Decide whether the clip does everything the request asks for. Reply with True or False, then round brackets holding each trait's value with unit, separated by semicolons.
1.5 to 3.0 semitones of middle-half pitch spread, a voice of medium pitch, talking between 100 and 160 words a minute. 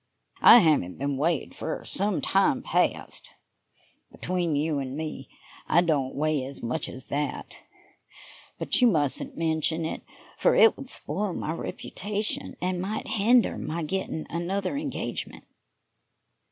False (5.0 semitones; 165 Hz; 135 wpm)